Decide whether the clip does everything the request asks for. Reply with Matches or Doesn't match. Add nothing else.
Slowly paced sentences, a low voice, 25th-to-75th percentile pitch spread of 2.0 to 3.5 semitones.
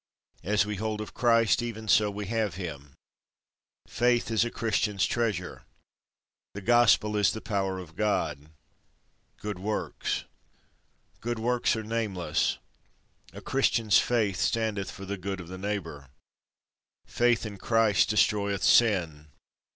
Matches